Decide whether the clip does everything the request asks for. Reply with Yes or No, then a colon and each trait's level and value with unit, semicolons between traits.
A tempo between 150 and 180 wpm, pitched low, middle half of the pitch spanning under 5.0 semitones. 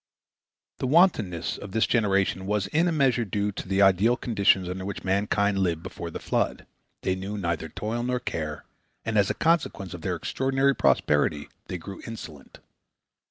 Yes: average, 170 wpm; low, 100 Hz; average, 4.3 semitones